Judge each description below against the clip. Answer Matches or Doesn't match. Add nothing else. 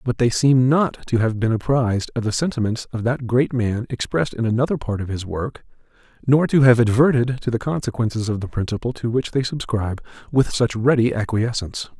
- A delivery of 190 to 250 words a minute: Matches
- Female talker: Doesn't match